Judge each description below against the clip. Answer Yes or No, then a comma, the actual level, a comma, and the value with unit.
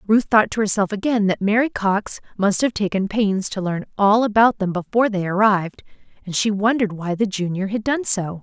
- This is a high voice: Yes, high, 205 Hz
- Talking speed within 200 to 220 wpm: Yes, fast, 205 wpm